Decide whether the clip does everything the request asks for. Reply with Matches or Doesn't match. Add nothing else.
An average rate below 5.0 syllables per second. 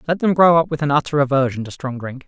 Doesn't match